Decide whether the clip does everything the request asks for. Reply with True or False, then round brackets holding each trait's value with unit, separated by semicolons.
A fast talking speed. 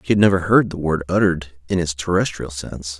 True (220 wpm)